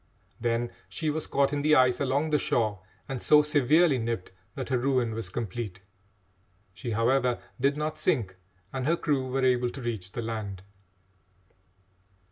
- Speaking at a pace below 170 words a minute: Yes, average, 160 wpm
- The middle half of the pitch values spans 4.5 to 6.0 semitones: No, average, 3.7 semitones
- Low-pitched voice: Yes, low, 125 Hz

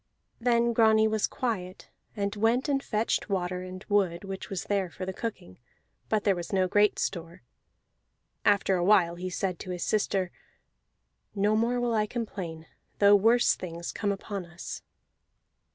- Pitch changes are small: No, average, 3.1 semitones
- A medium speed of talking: Yes, average, 160 wpm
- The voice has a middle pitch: No, high, 200 Hz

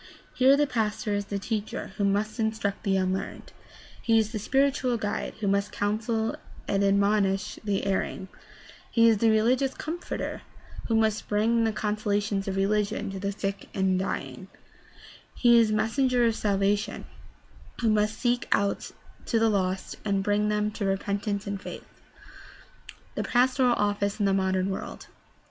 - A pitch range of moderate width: No, narrow, 2.1 semitones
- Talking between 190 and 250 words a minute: No, average, 160 wpm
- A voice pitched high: Yes, high, 210 Hz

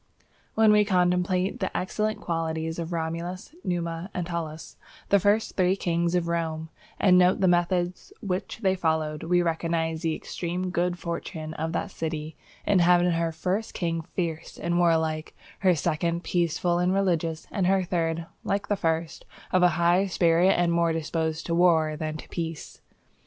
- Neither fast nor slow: Yes, average, 170 wpm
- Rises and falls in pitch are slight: Yes, narrow, 1.9 semitones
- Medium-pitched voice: Yes, medium, 170 Hz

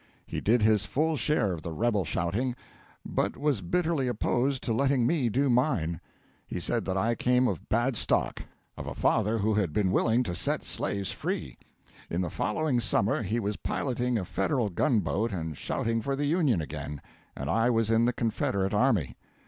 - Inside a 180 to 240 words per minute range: Yes, average, 190 wpm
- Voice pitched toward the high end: No, low, 115 Hz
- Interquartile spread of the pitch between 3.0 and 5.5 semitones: Yes, average, 4.5 semitones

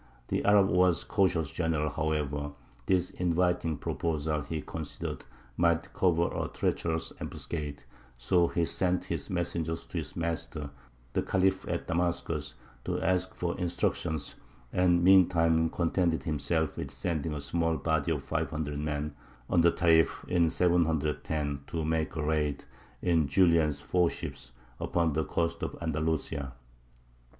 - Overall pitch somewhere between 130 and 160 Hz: No, very low, 80 Hz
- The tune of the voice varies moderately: No, narrow, 2.3 semitones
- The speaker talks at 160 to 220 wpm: No, slow, 135 wpm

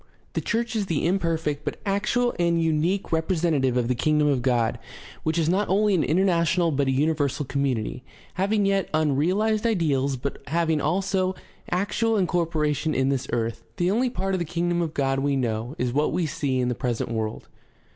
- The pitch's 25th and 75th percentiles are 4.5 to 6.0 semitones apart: Yes, wide, 5.6 semitones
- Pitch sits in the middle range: Yes, medium, 160 Hz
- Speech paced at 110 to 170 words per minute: No, average, 185 wpm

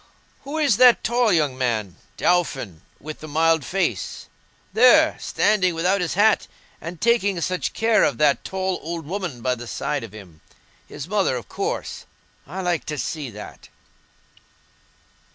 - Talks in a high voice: No, medium, 170 Hz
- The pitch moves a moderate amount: No, wide, 7.0 semitones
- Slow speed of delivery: No, average, 150 wpm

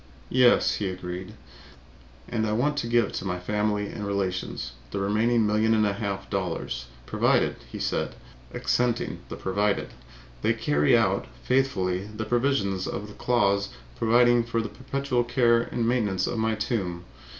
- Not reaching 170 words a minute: Yes, average, 150 wpm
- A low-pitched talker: Yes, low, 110 Hz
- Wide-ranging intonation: No, average, 3.4 semitones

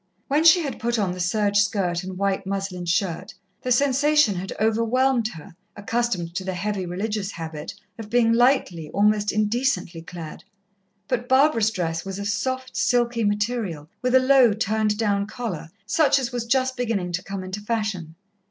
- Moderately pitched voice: No, high, 210 Hz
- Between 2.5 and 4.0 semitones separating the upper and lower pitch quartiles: No, average, 4.6 semitones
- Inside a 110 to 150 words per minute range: No, average, 170 wpm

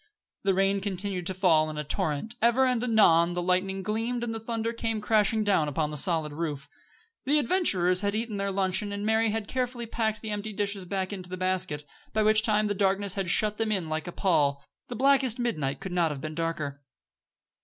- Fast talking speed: Yes, fast, 210 wpm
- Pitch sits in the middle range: No, high, 200 Hz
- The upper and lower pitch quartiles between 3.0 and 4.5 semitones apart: Yes, average, 4.1 semitones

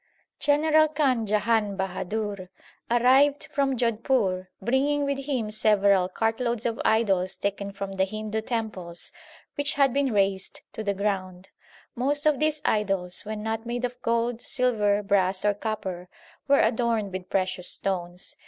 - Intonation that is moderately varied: Yes, average, 4.3 semitones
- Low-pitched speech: No, high, 215 Hz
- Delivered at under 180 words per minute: Yes, average, 145 wpm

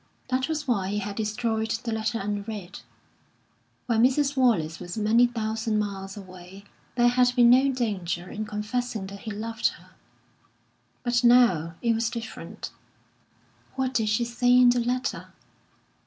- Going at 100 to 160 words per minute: Yes, average, 150 wpm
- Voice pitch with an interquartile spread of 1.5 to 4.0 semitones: Yes, average, 3.2 semitones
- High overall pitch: Yes, high, 225 Hz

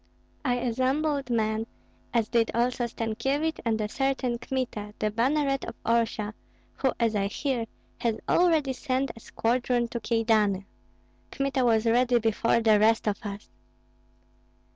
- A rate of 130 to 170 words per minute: Yes, average, 140 wpm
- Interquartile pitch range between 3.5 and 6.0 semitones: No, average, 2.9 semitones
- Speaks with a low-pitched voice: No, high, 235 Hz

